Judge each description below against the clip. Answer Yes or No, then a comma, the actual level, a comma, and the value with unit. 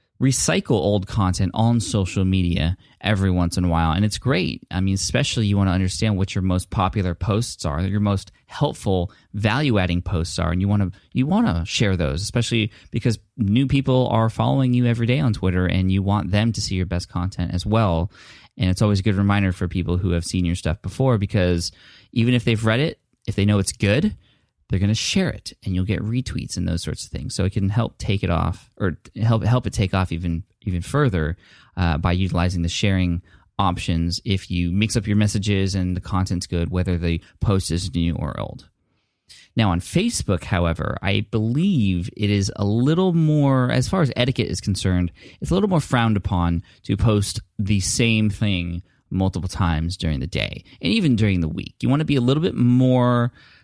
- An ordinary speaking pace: No, fast, 210 wpm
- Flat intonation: No, average, 4.1 semitones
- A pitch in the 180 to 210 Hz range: No, low, 100 Hz